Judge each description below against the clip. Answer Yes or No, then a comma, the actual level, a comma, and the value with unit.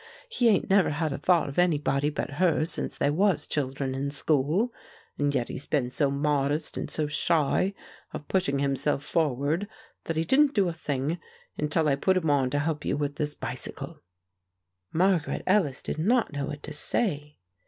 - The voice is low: No, medium, 150 Hz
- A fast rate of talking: No, average, 185 wpm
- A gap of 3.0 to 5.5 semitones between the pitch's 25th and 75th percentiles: Yes, average, 3.5 semitones